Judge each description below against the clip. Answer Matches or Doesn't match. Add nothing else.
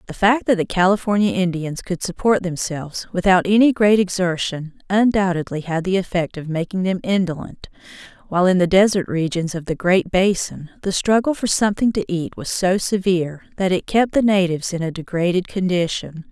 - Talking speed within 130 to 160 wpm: Doesn't match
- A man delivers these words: Doesn't match